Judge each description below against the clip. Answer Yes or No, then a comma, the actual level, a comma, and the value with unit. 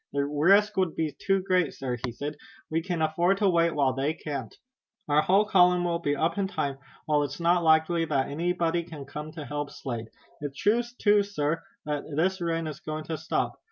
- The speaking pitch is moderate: Yes, medium, 160 Hz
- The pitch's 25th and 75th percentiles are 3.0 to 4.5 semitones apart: Yes, average, 3.4 semitones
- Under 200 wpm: No, fast, 205 wpm